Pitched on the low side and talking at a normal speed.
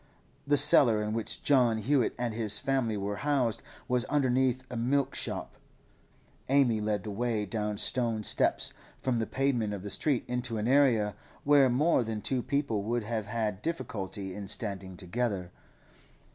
Yes: low, 115 Hz; average, 160 wpm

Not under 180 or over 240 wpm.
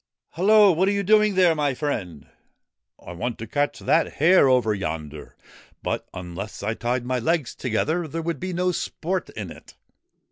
Yes: average, 190 wpm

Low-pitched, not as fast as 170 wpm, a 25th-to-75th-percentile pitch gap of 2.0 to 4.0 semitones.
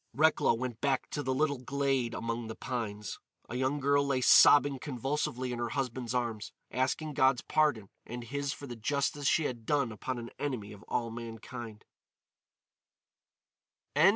Yes: low, 130 Hz; average, 155 wpm; average, 3.3 semitones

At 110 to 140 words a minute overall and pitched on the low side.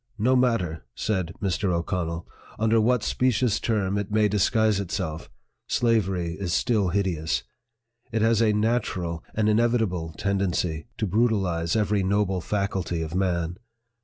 Yes: slow, 135 wpm; low, 100 Hz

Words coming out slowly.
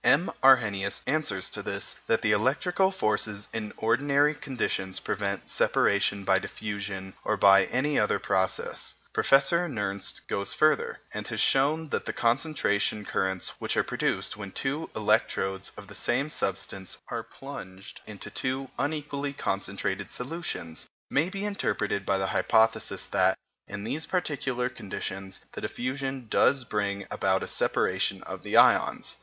No: average, 145 wpm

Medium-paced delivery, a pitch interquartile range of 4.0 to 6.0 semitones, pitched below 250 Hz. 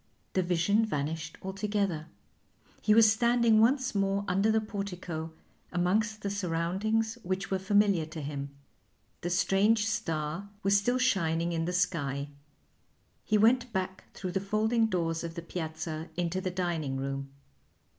Yes: average, 145 wpm; average, 4.4 semitones; high, 190 Hz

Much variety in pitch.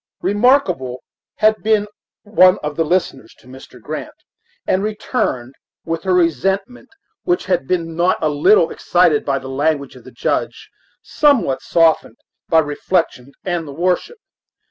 No: average, 5.0 semitones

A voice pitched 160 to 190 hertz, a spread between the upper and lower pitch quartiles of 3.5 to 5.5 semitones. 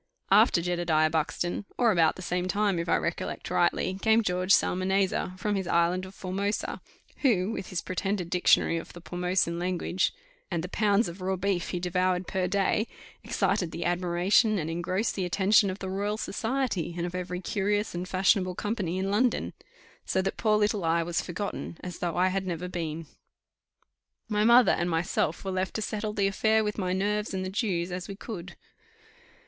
No: medium, 185 Hz; narrow, 2.6 semitones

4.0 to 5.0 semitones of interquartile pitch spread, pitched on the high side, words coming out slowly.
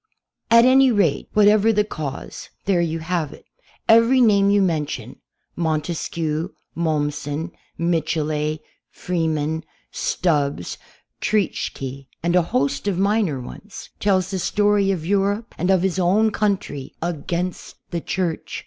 No: average, 4.5 semitones; medium, 175 Hz; slow, 130 wpm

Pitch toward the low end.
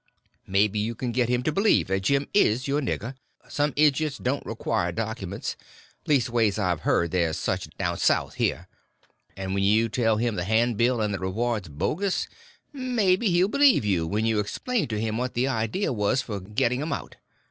Yes: low, 115 Hz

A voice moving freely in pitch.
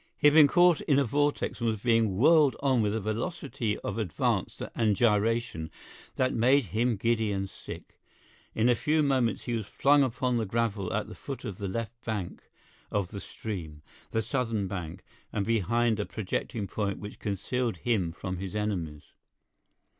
No: average, 3.7 semitones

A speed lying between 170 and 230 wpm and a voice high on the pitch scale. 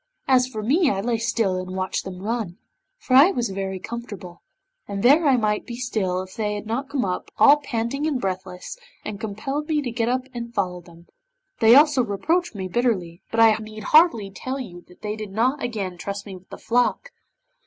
Yes: fast, 205 wpm; high, 225 Hz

